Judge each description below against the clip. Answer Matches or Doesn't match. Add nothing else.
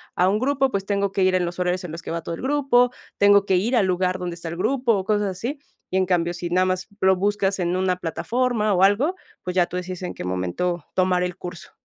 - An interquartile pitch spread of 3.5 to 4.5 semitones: Doesn't match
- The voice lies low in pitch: Doesn't match